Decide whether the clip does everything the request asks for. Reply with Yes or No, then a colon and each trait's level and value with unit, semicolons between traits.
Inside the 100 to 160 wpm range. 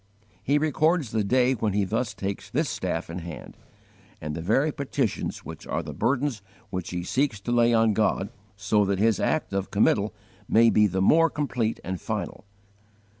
No: average, 180 wpm